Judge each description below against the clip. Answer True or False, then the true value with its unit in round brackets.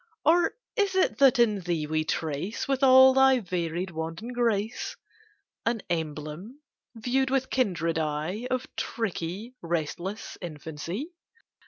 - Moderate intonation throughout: False (7.7 semitones)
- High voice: True (200 Hz)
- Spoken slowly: True (125 wpm)